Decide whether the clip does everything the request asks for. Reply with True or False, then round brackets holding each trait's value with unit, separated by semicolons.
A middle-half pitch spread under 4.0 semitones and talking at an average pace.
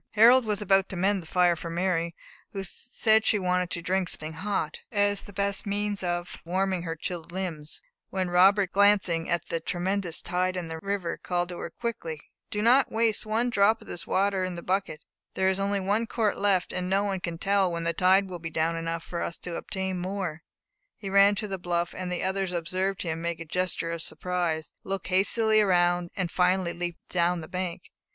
False (2.6 semitones; 210 wpm)